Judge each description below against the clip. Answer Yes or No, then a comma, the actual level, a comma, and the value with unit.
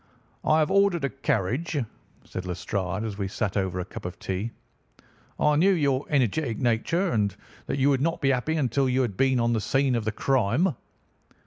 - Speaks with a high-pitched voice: No, low, 130 Hz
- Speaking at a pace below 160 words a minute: No, average, 195 wpm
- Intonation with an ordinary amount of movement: No, wide, 6.1 semitones